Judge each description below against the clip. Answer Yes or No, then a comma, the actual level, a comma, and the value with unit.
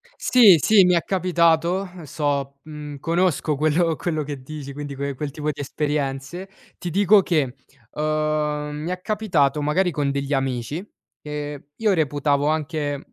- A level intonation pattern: No, average, 3.4 semitones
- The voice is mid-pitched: Yes, medium, 150 Hz